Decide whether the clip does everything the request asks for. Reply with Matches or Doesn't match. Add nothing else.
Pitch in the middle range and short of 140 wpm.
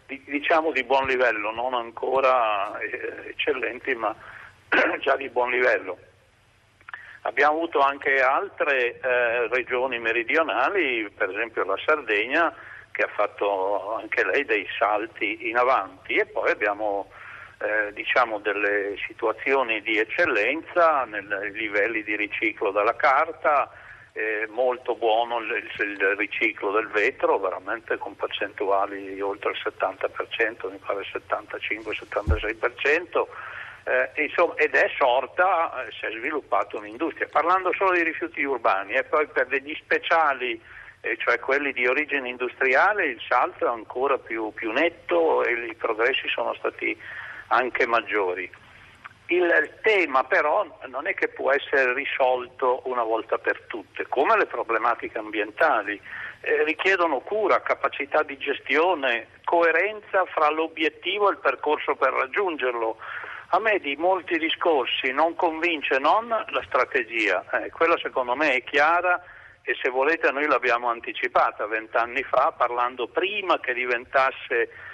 Matches